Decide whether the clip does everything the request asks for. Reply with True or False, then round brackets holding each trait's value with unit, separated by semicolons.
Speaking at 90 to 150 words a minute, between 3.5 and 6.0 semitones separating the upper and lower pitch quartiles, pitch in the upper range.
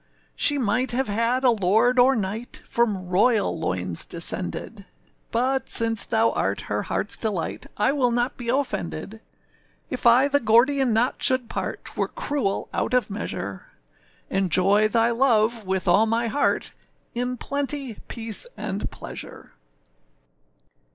True (140 wpm; 3.8 semitones; 230 Hz)